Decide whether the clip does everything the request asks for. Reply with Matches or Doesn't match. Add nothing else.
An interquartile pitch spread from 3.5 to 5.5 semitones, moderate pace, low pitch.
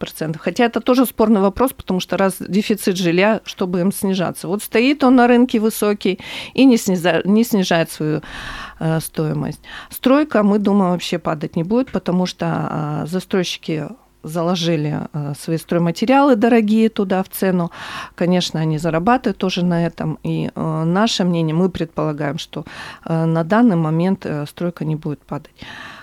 Doesn't match